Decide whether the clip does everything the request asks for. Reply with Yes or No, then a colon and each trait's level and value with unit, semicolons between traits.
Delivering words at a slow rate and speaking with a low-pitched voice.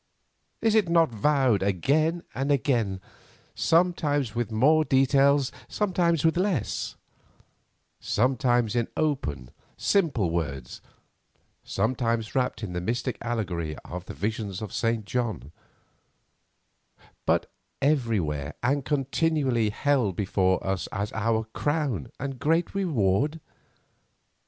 Yes: slow, 110 wpm; low, 120 Hz